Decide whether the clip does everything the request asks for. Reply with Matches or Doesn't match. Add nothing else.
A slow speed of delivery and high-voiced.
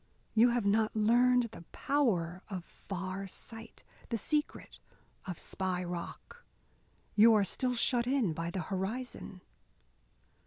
Matches